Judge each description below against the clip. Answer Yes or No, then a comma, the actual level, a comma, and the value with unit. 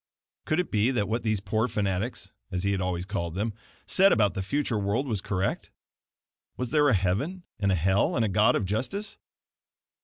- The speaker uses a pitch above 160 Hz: No, low, 105 Hz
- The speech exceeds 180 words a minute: Yes, average, 195 wpm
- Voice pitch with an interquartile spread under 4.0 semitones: No, average, 4.5 semitones